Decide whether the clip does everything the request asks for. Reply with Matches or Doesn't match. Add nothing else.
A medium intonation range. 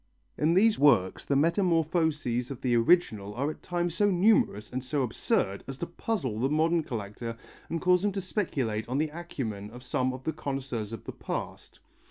Doesn't match